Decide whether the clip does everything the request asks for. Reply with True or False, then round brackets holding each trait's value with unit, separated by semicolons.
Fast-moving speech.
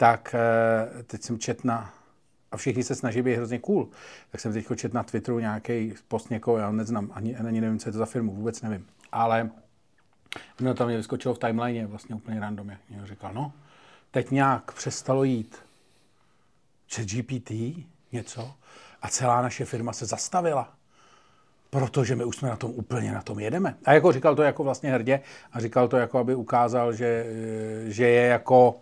True (180 wpm)